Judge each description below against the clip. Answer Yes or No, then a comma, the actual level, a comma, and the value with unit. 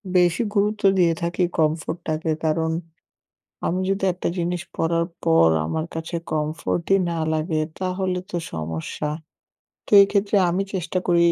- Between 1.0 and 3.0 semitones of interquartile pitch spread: Yes, narrow, 2.5 semitones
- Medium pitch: Yes, medium, 170 Hz